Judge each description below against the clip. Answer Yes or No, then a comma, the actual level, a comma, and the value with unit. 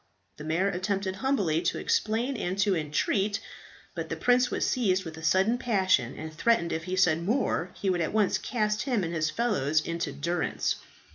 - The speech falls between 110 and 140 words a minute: No, average, 190 wpm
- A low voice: No, medium, 185 Hz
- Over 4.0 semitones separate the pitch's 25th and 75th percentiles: Yes, average, 4.6 semitones